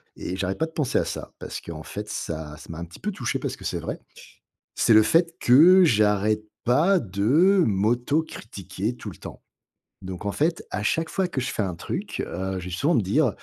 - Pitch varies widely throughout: Yes, wide, 8.7 semitones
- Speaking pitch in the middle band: No, low, 110 Hz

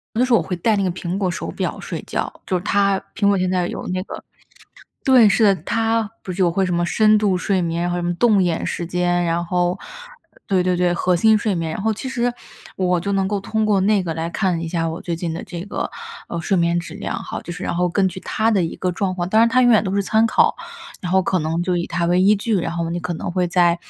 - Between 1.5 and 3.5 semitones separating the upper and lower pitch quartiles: Yes, average, 2.8 semitones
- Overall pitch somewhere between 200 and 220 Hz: No, medium, 185 Hz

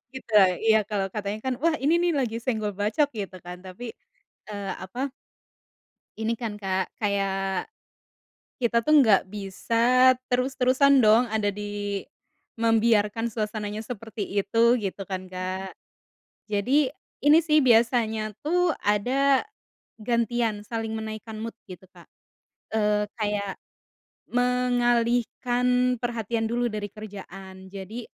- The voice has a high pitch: Yes, high, 220 Hz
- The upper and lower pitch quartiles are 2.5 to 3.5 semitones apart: Yes, average, 3.2 semitones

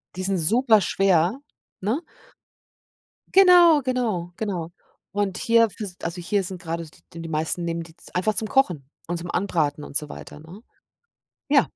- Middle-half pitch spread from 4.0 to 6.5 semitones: Yes, average, 4.6 semitones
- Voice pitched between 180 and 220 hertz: Yes, medium, 185 Hz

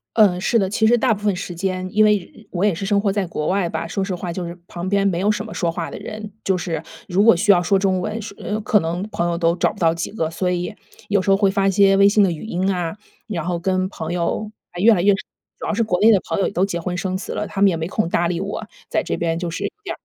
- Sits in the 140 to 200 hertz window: Yes, high, 190 Hz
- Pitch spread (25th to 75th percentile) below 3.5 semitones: Yes, average, 2.8 semitones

